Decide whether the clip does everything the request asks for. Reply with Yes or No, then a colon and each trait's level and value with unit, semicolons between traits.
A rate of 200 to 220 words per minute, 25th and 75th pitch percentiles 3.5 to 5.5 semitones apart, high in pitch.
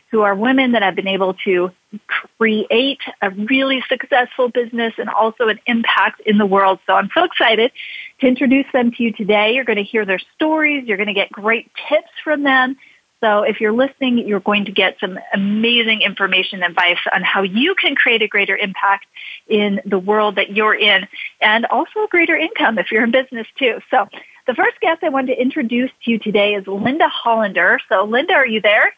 Yes: fast, 205 wpm; average, 4.5 semitones; high, 225 Hz